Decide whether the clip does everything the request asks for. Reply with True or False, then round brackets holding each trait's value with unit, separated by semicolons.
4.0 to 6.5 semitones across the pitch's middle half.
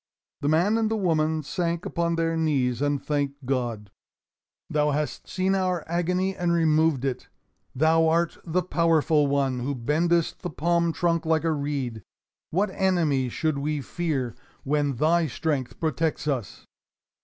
False (3.2 semitones)